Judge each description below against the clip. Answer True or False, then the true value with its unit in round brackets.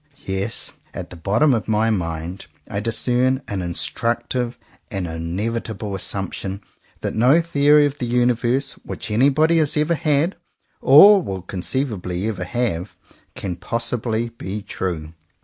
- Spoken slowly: True (130 wpm)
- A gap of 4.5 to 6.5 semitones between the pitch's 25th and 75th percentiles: True (5.6 semitones)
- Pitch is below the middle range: True (115 Hz)